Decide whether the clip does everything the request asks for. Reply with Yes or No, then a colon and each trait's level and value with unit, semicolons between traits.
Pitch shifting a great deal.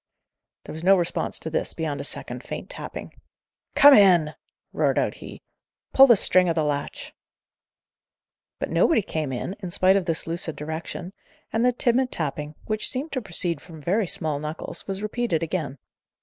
No: average, 4.8 semitones